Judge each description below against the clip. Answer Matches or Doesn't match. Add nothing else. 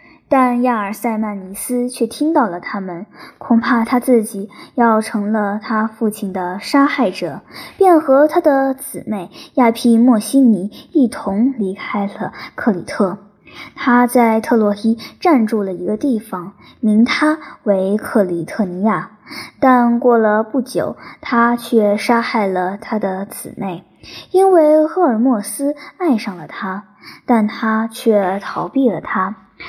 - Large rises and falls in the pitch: Doesn't match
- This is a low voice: Doesn't match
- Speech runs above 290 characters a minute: Doesn't match